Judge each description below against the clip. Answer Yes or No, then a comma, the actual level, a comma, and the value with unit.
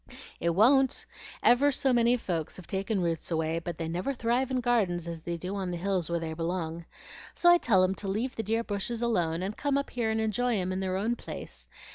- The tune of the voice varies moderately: No, wide, 5.7 semitones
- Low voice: No, high, 195 Hz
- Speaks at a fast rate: Yes, fast, 230 wpm